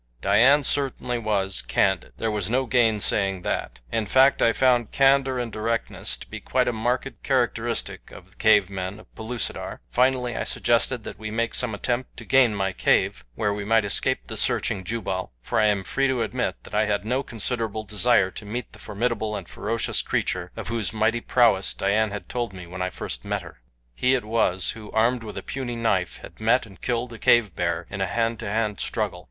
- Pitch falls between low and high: No, low, 110 Hz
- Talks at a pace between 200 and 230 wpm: Yes, fast, 205 wpm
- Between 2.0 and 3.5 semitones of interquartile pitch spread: Yes, average, 3.2 semitones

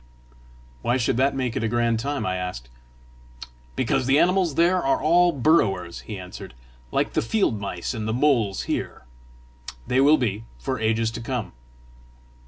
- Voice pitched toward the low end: Yes, low, 120 Hz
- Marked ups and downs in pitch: No, average, 4.7 semitones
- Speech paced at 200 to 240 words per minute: No, average, 170 wpm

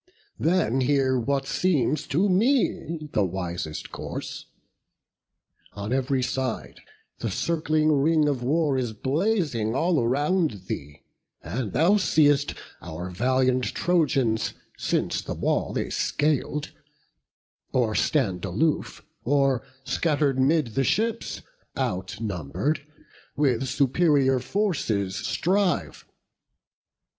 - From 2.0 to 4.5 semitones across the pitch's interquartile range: No, average, 5.2 semitones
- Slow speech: Yes, slow, 100 wpm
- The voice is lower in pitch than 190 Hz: Yes, low, 135 Hz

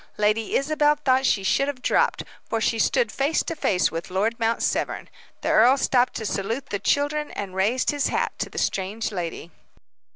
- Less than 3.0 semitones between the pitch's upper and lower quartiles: No, wide, 5.4 semitones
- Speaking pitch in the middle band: No, high, 230 Hz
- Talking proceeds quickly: No, average, 190 wpm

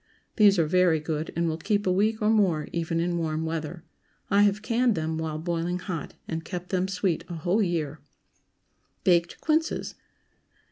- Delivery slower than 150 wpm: No, average, 175 wpm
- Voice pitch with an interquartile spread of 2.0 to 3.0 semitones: No, average, 3.5 semitones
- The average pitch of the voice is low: No, medium, 175 Hz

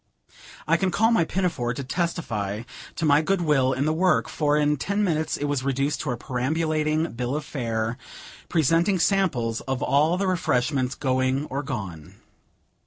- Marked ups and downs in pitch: No, average, 4.5 semitones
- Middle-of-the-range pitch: Yes, medium, 145 Hz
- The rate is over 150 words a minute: Yes, average, 170 wpm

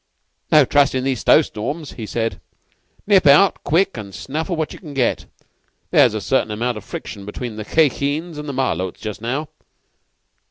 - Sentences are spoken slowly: No, average, 175 wpm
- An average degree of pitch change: No, wide, 6.0 semitones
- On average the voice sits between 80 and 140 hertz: Yes, low, 135 Hz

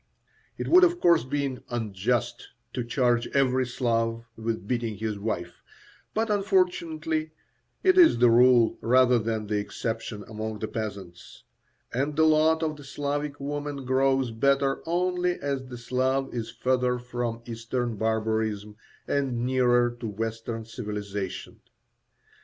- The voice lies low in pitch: Yes, low, 125 Hz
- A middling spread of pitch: Yes, average, 4.0 semitones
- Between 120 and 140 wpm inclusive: Yes, slow, 135 wpm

